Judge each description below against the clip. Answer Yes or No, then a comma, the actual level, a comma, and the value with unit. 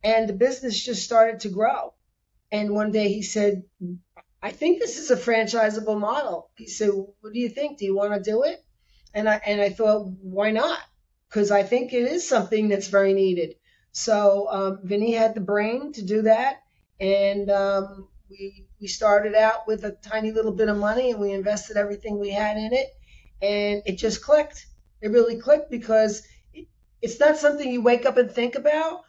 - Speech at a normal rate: Yes, average, 195 wpm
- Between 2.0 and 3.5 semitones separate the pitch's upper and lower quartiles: Yes, average, 3.0 semitones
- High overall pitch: Yes, high, 215 Hz